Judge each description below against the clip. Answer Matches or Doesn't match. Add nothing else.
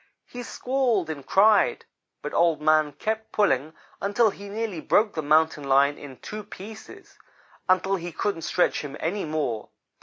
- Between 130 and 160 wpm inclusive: Matches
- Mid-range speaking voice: Matches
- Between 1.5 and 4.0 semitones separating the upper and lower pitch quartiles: Doesn't match